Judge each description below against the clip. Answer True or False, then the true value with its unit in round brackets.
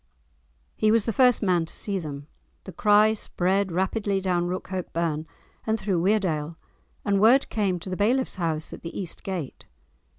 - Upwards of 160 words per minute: True (170 wpm)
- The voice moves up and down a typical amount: True (3.7 semitones)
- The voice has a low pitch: False (190 Hz)